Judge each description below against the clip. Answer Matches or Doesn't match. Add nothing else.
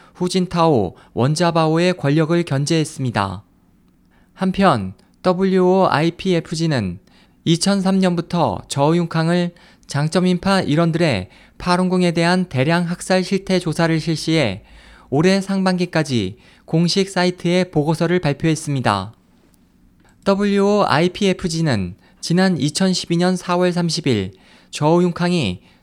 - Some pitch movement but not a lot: Matches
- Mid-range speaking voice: Matches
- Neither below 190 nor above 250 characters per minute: Matches